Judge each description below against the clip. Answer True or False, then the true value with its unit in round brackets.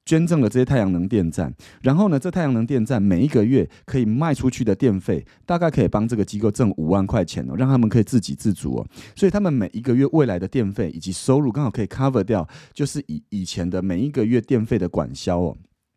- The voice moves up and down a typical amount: False (6.2 semitones)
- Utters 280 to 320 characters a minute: False (370 characters per minute)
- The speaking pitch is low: True (115 Hz)